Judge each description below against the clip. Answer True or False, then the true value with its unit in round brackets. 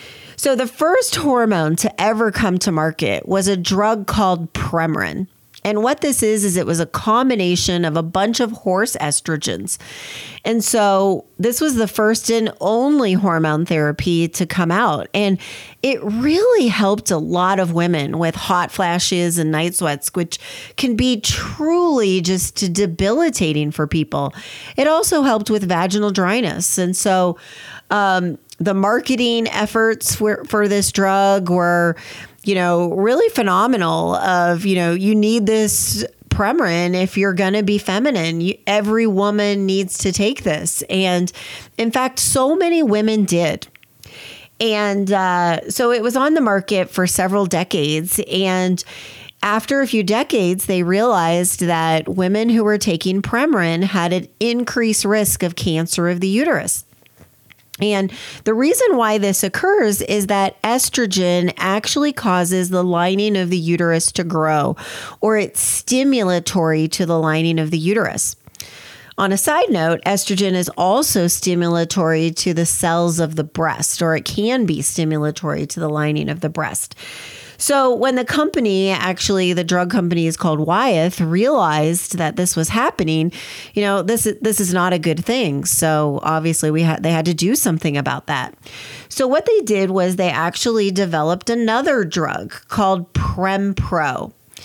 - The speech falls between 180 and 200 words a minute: False (155 wpm)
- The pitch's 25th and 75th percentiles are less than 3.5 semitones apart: False (4.2 semitones)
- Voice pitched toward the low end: False (190 Hz)